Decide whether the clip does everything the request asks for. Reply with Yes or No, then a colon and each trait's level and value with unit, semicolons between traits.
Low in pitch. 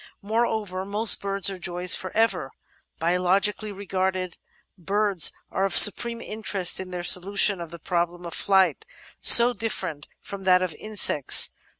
No: high, 190 Hz